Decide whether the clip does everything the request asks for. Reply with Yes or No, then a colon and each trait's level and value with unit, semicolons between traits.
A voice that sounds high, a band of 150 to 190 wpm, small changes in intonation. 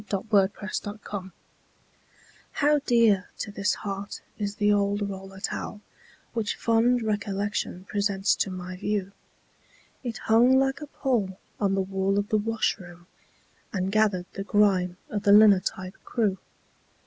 No: high, 205 Hz; average, 140 wpm; narrow, 2.1 semitones